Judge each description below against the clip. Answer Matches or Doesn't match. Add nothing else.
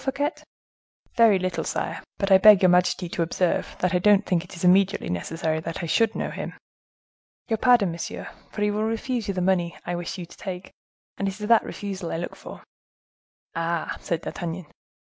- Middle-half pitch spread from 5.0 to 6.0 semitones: Doesn't match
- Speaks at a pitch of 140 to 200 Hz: Matches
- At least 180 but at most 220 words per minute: Matches